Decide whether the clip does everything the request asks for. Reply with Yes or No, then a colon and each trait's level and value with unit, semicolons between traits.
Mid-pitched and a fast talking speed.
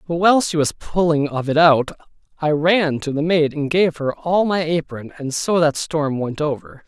Yes: medium, 155 Hz; fast, 220 wpm